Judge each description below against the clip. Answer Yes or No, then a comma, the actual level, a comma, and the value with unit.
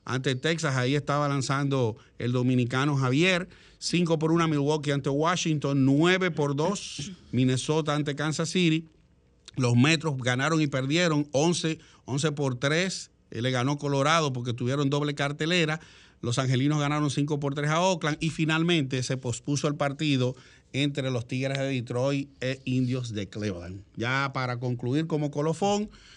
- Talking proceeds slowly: No, average, 145 wpm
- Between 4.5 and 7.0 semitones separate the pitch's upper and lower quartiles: No, average, 3.5 semitones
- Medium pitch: Yes, medium, 145 Hz